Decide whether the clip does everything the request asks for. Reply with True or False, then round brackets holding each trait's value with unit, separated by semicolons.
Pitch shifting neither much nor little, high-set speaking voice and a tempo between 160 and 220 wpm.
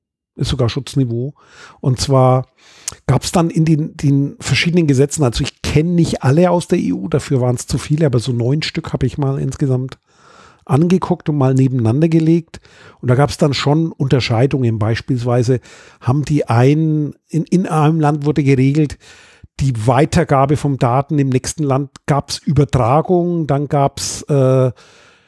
False (3.0 semitones; 140 Hz; 165 wpm)